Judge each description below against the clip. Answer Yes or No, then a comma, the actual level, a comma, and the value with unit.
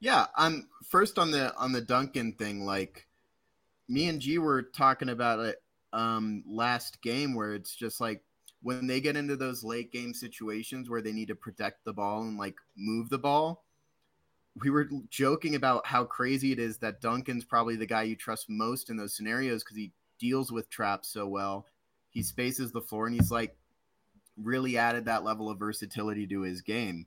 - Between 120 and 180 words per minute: No, average, 195 wpm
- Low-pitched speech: Yes, low, 115 Hz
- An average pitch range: Yes, average, 3.1 semitones